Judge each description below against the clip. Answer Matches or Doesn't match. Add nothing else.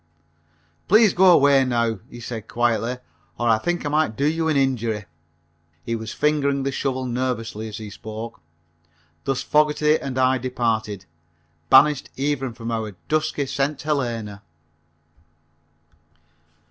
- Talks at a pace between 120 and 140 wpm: Matches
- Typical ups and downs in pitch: Matches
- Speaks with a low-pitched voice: Matches